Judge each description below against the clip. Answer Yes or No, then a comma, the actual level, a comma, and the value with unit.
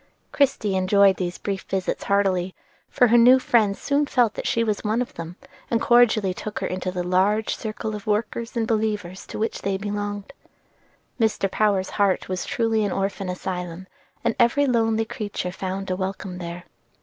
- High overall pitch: Yes, high, 205 Hz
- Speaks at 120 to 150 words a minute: No, average, 175 wpm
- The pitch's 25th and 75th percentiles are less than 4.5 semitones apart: Yes, average, 3.2 semitones